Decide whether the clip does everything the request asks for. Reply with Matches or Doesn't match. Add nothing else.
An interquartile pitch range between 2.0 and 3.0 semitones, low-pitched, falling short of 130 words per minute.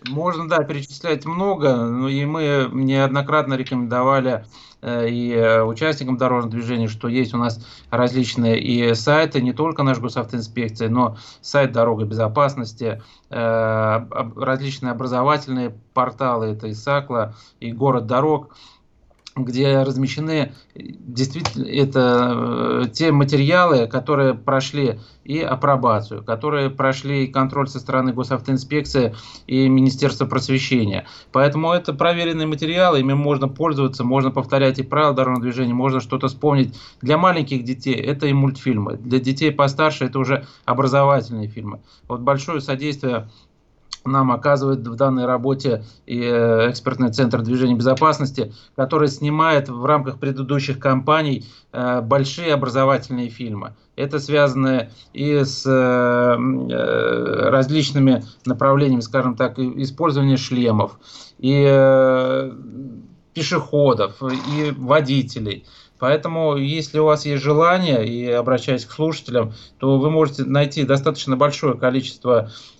Matches